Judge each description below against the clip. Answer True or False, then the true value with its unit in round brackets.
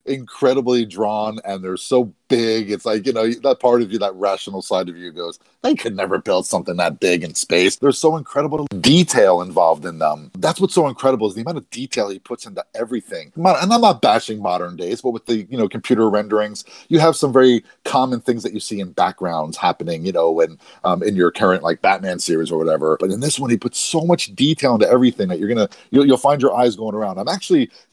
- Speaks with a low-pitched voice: True (115 Hz)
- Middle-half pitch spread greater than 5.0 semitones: True (5.4 semitones)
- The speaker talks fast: True (235 wpm)